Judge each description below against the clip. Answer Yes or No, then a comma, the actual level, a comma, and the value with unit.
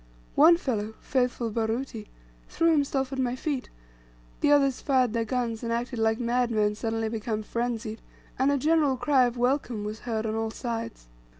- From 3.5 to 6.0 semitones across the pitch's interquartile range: No, average, 3.0 semitones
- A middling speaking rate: Yes, average, 170 wpm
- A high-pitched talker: Yes, high, 240 Hz